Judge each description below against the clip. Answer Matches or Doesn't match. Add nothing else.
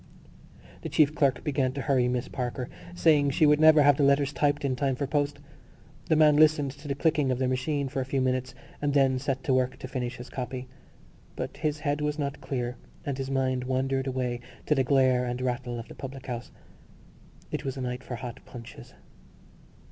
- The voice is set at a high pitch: Doesn't match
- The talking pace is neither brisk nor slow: Doesn't match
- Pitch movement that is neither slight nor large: Doesn't match